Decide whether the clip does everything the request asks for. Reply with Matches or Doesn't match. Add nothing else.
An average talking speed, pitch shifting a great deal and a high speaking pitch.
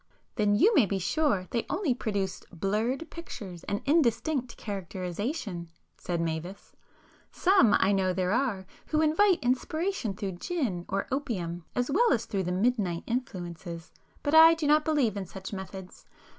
Matches